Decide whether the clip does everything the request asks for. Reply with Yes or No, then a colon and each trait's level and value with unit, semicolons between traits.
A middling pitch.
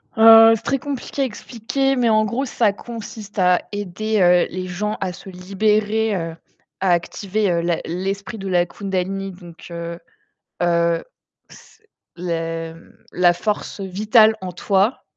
No: high, 195 Hz